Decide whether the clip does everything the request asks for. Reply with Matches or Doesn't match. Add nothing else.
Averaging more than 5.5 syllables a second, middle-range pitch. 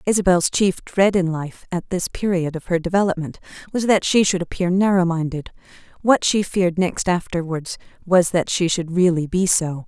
Doesn't match